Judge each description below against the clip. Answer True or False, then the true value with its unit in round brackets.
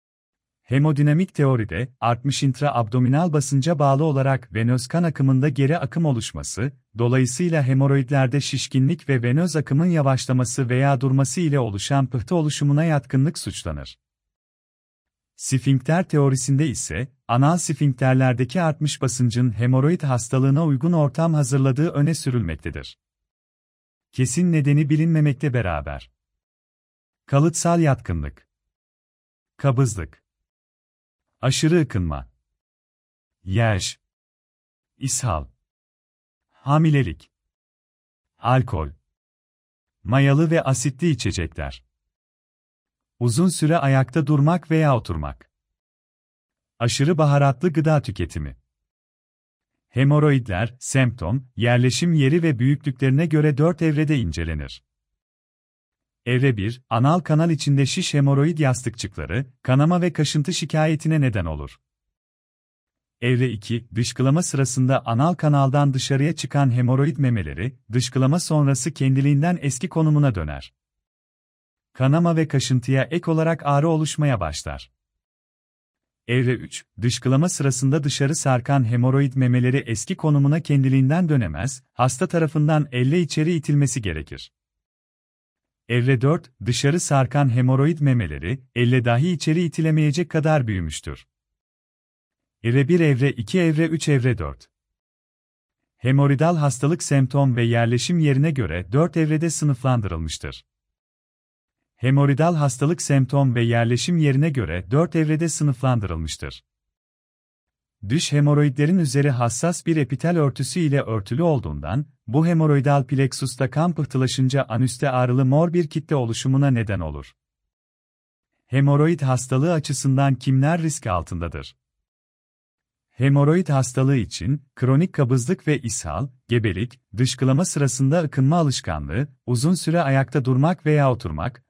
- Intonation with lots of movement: True (8.9 semitones)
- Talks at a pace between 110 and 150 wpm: False (100 wpm)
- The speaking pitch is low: True (130 Hz)